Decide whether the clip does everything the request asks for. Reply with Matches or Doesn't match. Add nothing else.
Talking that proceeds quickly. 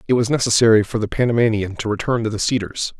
Matches